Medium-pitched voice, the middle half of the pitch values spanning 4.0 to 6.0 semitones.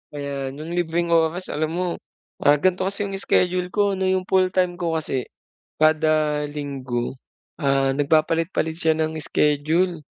No: medium, 160 Hz; average, 3.5 semitones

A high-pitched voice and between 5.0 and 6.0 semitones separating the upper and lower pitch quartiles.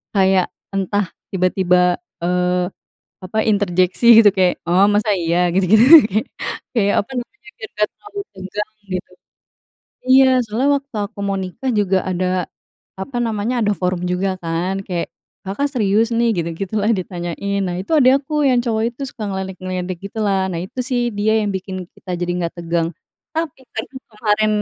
No: high, 195 Hz; average, 3.5 semitones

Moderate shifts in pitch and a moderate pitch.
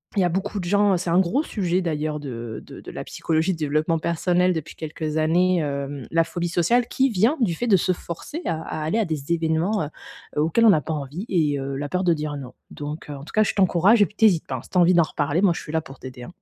Yes: average, 3.6 semitones; medium, 165 Hz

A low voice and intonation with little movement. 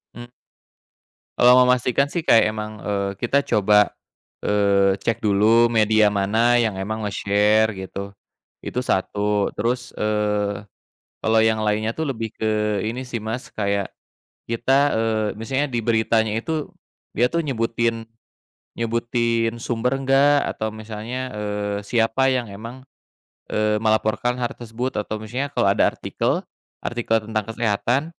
Yes: low, 110 Hz; narrow, 2.3 semitones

